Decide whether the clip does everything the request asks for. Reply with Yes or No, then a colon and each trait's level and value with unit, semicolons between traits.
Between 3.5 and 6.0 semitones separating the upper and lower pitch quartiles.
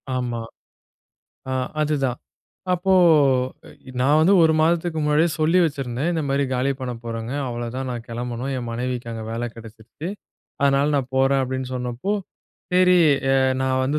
Yes: average, 3.9 semitones